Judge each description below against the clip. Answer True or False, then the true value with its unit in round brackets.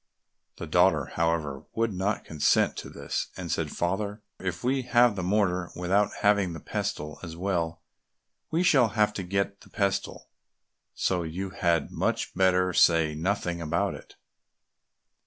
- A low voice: True (95 Hz)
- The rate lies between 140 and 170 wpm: True (150 wpm)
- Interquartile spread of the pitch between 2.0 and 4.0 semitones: True (3.5 semitones)